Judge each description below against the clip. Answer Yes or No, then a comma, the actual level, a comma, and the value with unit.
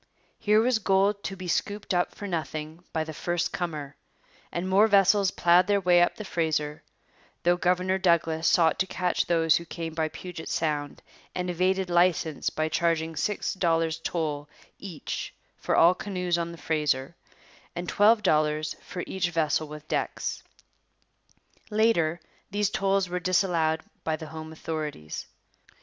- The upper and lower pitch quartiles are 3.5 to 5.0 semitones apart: No, average, 3.0 semitones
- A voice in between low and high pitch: Yes, medium, 170 Hz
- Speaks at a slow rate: No, average, 155 wpm